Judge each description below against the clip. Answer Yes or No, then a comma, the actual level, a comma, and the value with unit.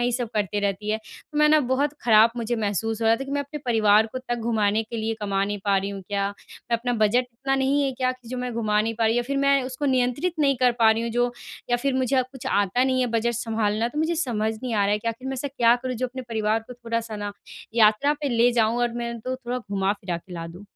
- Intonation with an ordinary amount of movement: Yes, average, 3.1 semitones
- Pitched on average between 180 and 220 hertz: No, high, 235 Hz